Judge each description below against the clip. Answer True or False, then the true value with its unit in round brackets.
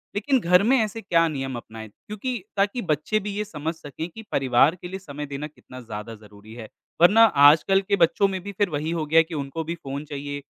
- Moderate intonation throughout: False (6.1 semitones)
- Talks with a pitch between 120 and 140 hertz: False (160 Hz)